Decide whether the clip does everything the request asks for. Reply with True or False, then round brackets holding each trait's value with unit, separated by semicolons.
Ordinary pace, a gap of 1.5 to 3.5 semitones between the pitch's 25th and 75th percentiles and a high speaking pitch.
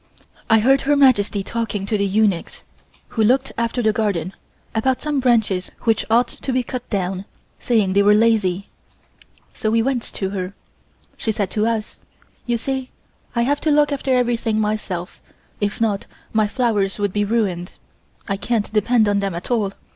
True (175 wpm; 3.2 semitones; 220 Hz)